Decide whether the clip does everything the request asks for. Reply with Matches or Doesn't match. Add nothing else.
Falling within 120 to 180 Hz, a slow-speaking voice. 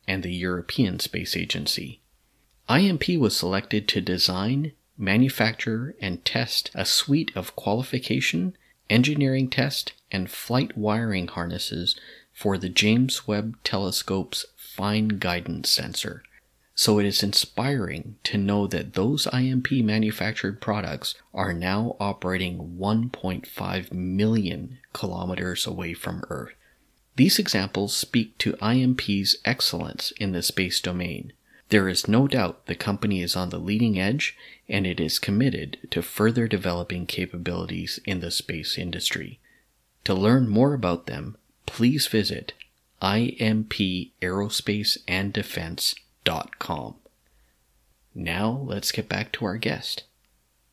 Doesn't match